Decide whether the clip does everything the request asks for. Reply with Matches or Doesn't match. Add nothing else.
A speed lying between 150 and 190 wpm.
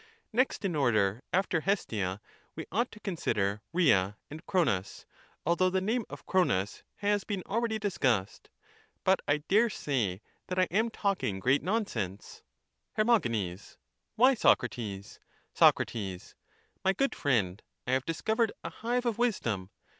Doesn't match